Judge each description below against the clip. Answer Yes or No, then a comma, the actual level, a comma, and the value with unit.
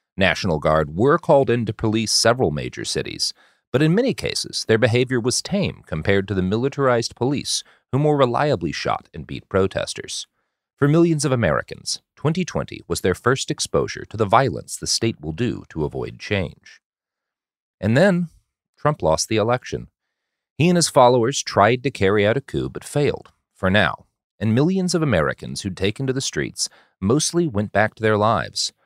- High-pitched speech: No, low, 120 Hz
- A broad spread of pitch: Yes, wide, 5.7 semitones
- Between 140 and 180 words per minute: Yes, average, 175 wpm